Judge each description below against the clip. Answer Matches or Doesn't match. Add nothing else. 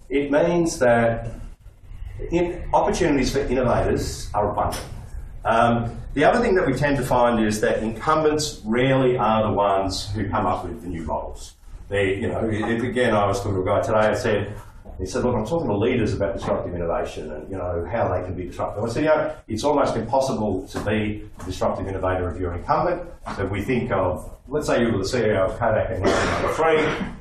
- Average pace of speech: Doesn't match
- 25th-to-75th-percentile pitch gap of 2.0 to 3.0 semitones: Doesn't match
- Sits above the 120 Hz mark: Doesn't match